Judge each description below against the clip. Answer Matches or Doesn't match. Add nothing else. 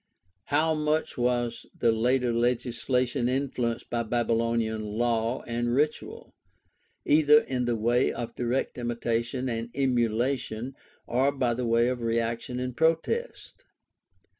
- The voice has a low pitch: Matches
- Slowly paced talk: Matches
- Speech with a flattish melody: Matches